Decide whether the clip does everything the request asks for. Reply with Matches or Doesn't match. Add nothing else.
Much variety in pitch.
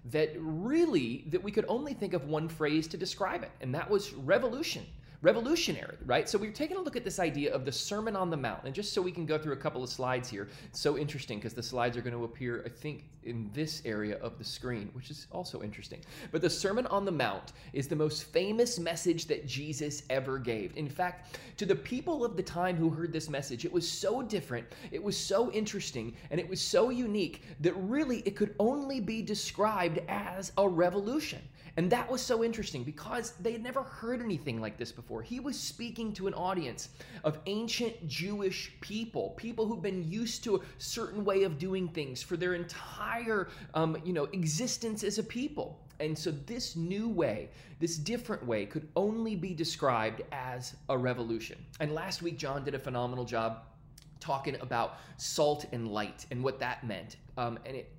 Matches